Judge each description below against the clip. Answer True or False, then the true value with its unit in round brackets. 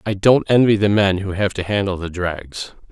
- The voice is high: False (100 Hz)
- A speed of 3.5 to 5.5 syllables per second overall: True (4.9 syllables/s)